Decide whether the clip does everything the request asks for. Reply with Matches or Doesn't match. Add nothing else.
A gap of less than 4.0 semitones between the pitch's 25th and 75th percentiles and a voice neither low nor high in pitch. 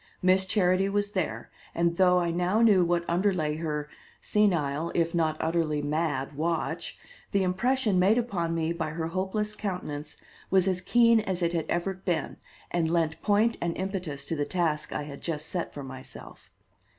Matches